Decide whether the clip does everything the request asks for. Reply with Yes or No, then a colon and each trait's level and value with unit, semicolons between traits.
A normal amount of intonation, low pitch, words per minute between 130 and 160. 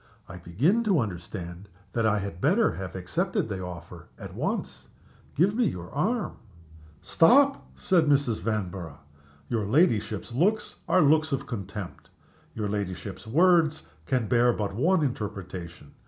No: wide, 8.8 semitones; low, 110 Hz; average, 140 wpm